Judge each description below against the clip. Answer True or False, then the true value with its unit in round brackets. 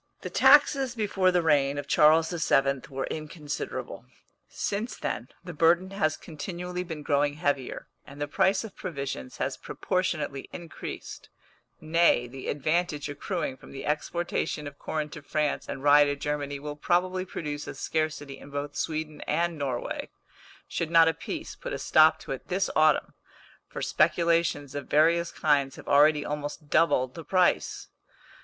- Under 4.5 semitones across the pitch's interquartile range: True (3.1 semitones)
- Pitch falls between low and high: True (155 Hz)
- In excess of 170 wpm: False (155 wpm)